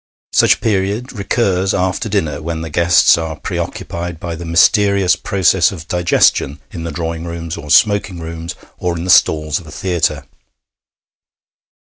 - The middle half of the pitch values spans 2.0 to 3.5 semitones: Yes, average, 2.8 semitones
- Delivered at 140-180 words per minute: Yes, average, 155 wpm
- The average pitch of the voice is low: Yes, very low, 85 Hz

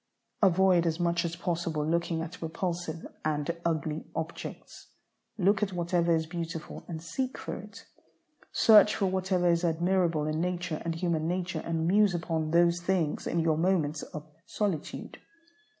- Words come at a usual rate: Yes, average, 150 wpm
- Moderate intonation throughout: No, narrow, 1.9 semitones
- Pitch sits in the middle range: Yes, medium, 170 Hz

